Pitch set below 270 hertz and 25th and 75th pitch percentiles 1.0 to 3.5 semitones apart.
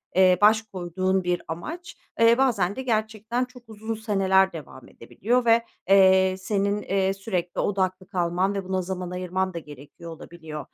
Yes: high, 190 Hz; average, 3.2 semitones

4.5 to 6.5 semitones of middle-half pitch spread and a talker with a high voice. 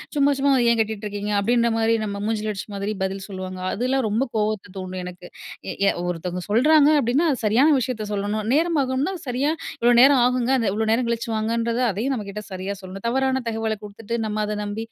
No: average, 3.8 semitones; high, 220 Hz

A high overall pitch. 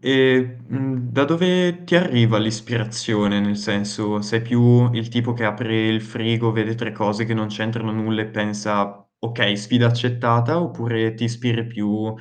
No: low, 115 Hz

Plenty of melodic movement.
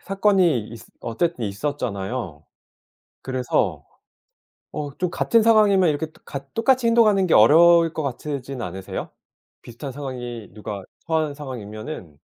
Yes: wide, 6.8 semitones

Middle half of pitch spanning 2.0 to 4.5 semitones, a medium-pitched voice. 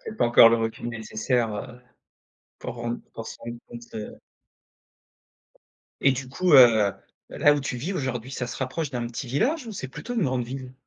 No: average, 2.8 semitones; low, 125 Hz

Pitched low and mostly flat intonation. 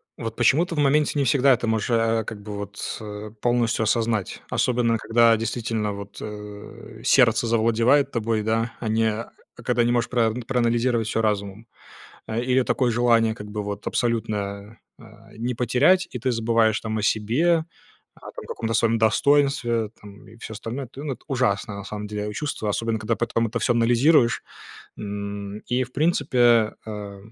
Yes: low, 115 Hz; narrow, 2.3 semitones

